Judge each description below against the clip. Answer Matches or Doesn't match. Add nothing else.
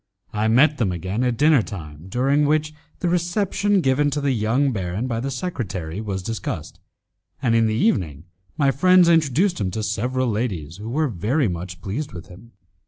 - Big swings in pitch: Matches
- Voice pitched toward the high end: Doesn't match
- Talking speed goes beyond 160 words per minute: Matches